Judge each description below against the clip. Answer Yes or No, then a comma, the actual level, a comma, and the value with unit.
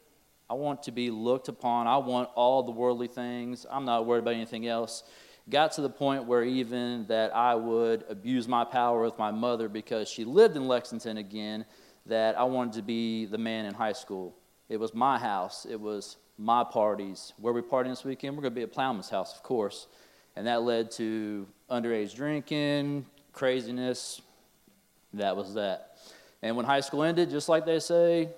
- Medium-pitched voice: No, low, 120 Hz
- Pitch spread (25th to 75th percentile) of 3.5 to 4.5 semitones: No, average, 3.1 semitones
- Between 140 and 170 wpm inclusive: No, average, 190 wpm